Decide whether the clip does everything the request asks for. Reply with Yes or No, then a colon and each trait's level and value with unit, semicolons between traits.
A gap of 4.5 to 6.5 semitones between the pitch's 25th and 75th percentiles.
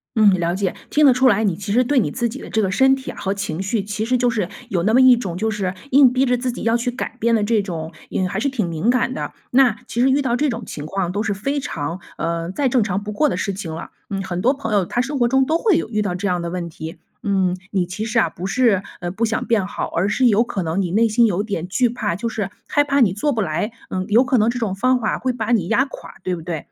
Yes: average, 4.9 semitones